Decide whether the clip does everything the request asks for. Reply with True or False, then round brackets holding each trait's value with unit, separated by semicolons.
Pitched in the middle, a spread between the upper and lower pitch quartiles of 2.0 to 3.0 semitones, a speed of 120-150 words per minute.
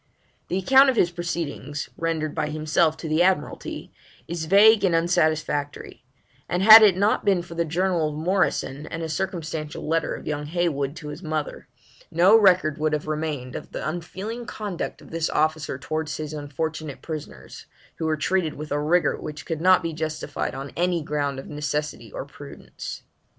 False (160 Hz; 2.7 semitones; 175 wpm)